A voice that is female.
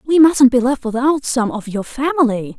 Yes: female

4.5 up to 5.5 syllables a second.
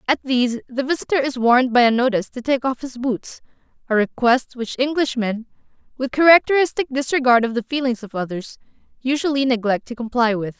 No: 5.8 syllables/s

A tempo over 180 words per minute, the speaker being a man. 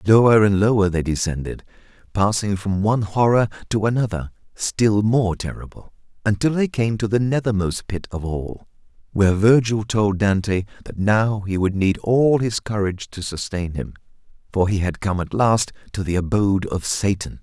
No: average, 170 wpm; male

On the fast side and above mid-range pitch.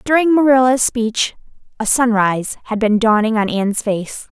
No: average, 150 wpm; high, 230 Hz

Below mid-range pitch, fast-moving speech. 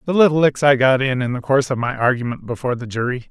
Yes: low, 130 Hz; fast, 270 wpm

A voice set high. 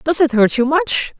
Yes: very high, 290 Hz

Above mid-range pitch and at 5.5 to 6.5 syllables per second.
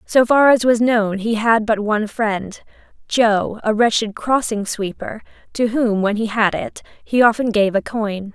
No: high, 220 Hz; 4.2 syllables/s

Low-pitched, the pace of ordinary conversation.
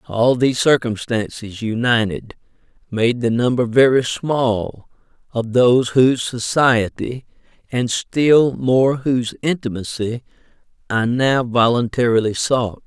No: low, 120 Hz; slow, 105 wpm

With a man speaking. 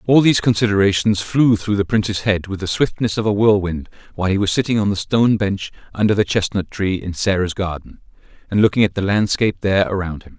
Yes: male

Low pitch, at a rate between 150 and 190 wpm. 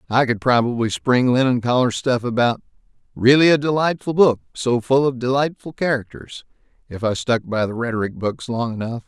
Yes: low, 125 Hz; average, 170 wpm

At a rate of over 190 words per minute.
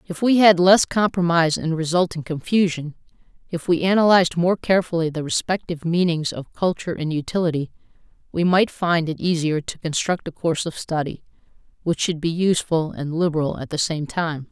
No: average, 170 wpm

